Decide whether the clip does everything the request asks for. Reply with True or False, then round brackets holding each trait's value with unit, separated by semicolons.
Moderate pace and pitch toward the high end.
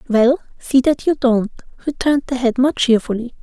True (175 wpm; 255 Hz)